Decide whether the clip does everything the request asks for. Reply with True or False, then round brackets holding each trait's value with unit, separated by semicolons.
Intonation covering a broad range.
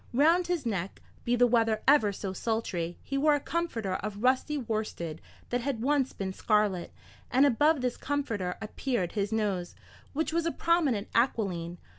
True (6.0 semitones)